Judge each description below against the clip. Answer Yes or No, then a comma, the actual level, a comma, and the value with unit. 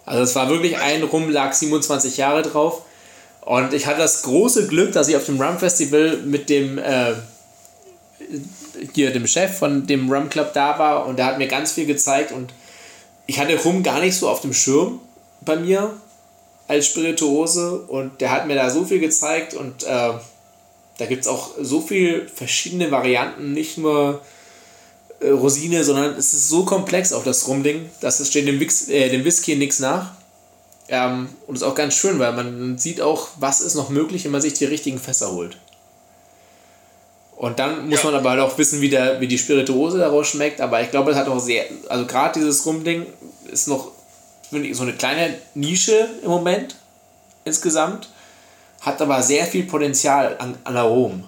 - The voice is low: No, medium, 145 Hz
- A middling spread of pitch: Yes, average, 3.7 semitones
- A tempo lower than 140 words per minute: No, average, 185 wpm